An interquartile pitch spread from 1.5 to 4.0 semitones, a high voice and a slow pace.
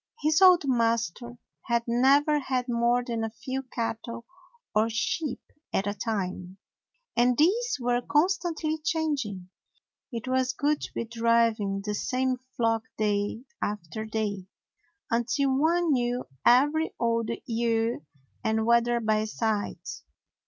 Yes: average, 3.2 semitones; high, 235 Hz; slow, 125 wpm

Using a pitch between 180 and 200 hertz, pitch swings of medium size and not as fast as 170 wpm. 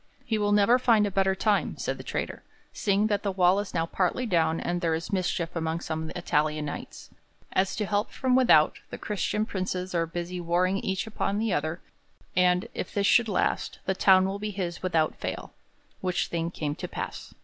No: medium, 185 Hz; average, 3.3 semitones; average, 200 wpm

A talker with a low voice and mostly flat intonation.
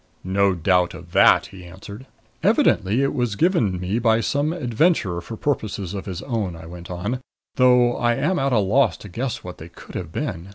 No: low, 105 Hz; wide, 5.5 semitones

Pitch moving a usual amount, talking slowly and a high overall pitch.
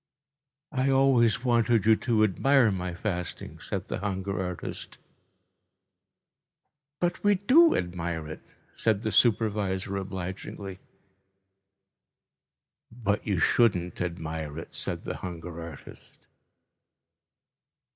No: average, 4.9 semitones; slow, 100 wpm; low, 100 Hz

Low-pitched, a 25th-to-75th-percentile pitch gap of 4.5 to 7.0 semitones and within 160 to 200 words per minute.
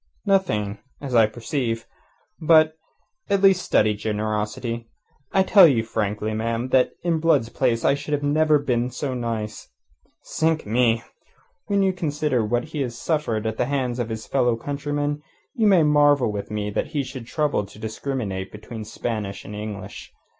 Yes: low, 120 Hz; average, 5.2 semitones; average, 165 wpm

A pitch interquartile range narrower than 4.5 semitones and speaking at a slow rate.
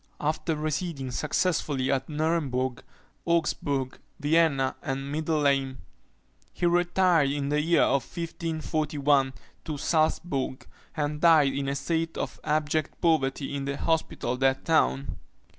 Yes: average, 2.9 semitones; slow, 120 wpm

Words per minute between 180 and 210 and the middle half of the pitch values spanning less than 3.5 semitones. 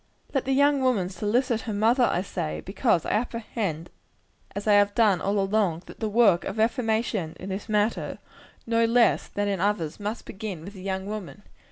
Yes: average, 190 wpm; average, 3.1 semitones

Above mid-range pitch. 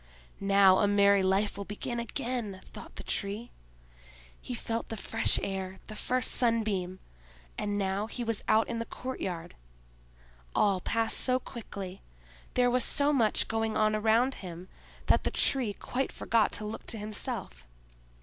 Yes: high, 210 Hz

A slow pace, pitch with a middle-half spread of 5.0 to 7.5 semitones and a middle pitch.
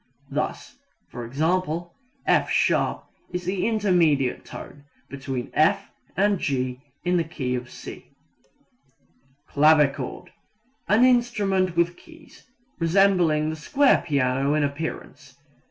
Yes: slow, 105 wpm; wide, 5.5 semitones; medium, 160 Hz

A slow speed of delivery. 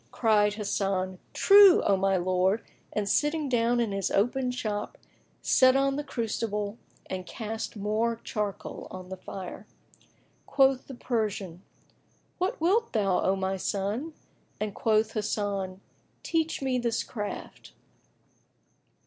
Yes: slow, 125 wpm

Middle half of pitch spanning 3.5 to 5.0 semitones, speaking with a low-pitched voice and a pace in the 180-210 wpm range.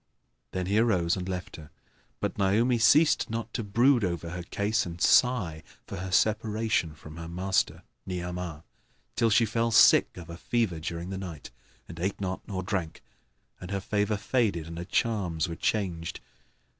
No: average, 4.3 semitones; very low, 95 Hz; average, 170 wpm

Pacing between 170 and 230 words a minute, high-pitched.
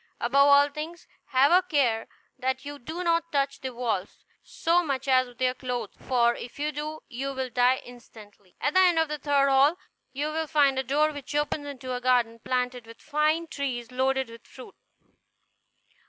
Yes: average, 190 wpm; very high, 270 Hz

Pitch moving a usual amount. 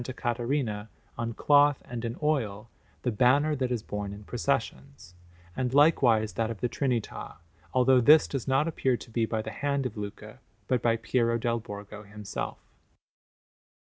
Yes: average, 3.5 semitones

